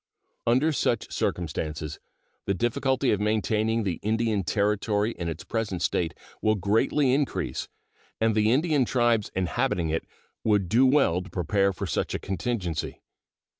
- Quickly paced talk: No, average, 140 wpm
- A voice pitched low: Yes, low, 105 Hz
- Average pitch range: Yes, average, 4.5 semitones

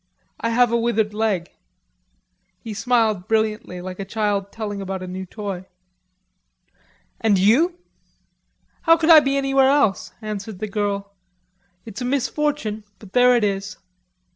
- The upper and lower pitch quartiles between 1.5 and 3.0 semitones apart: No, average, 3.8 semitones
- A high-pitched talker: Yes, high, 215 Hz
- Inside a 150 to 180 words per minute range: No, average, 140 wpm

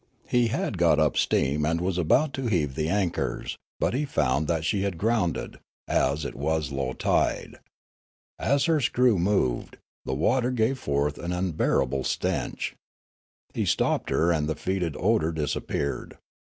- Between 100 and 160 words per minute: Yes, average, 155 wpm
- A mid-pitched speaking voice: No, very low, 85 Hz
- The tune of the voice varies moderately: No, wide, 6.7 semitones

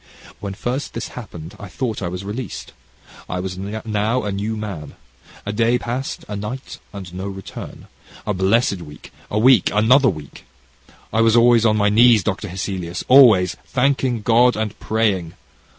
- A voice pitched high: No, low, 105 Hz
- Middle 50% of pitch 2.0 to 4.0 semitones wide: Yes, average, 3.6 semitones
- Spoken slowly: No, average, 165 wpm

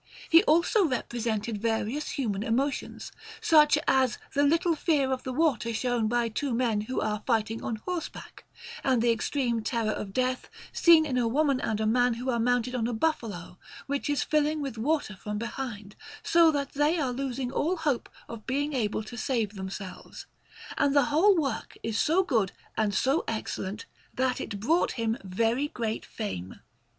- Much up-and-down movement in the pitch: No, average, 4.5 semitones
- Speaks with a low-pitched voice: No, high, 245 Hz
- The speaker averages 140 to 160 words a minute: No, average, 175 wpm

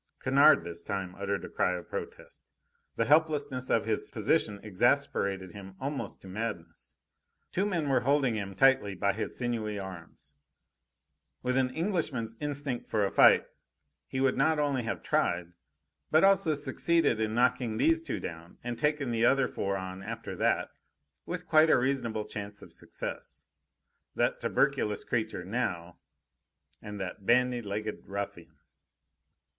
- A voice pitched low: Yes, low, 115 Hz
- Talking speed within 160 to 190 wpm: No, average, 150 wpm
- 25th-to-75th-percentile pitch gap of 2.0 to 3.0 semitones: No, wide, 5.5 semitones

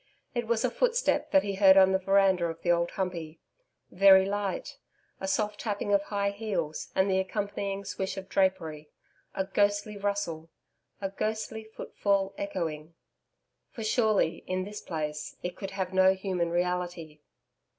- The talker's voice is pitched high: Yes, high, 195 Hz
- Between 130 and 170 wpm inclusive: Yes, average, 155 wpm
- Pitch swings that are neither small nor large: No, narrow, 2.3 semitones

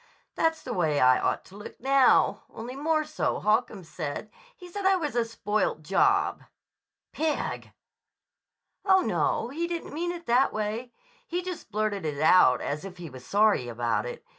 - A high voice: Yes, high, 225 Hz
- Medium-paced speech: Yes, average, 170 wpm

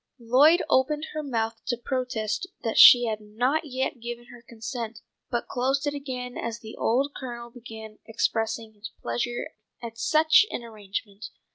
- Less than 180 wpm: Yes, average, 155 wpm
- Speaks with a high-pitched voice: Yes, high, 235 Hz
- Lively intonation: No, average, 2.7 semitones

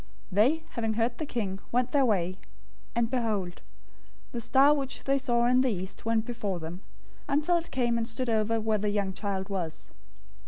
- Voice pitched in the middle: No, high, 230 Hz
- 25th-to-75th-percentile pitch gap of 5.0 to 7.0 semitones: No, average, 4.2 semitones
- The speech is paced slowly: No, average, 190 wpm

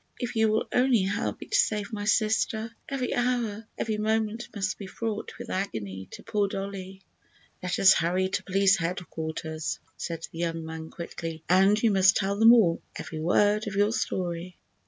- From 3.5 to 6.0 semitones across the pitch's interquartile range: Yes, average, 3.9 semitones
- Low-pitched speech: No, high, 195 Hz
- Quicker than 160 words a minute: Yes, average, 175 wpm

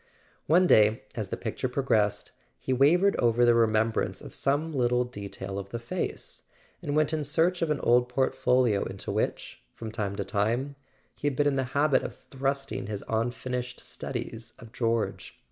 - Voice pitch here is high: No, low, 125 Hz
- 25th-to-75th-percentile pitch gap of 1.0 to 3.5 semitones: No, average, 3.9 semitones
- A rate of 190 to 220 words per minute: No, average, 175 wpm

